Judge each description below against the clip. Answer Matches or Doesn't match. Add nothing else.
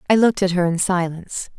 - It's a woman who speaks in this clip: Matches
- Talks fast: Matches